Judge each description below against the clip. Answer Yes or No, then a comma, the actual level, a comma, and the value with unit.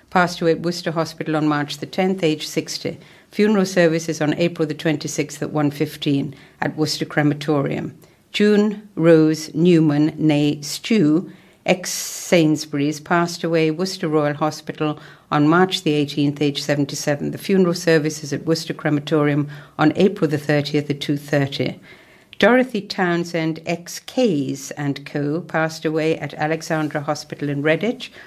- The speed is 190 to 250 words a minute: No, slow, 135 wpm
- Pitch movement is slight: Yes, narrow, 2.3 semitones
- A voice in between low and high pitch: Yes, medium, 155 Hz